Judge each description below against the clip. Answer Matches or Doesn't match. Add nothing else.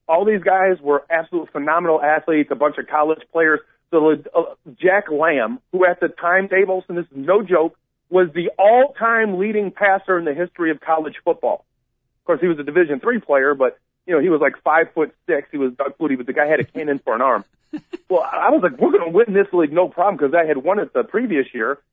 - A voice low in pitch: Doesn't match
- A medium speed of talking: Doesn't match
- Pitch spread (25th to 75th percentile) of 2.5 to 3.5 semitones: Doesn't match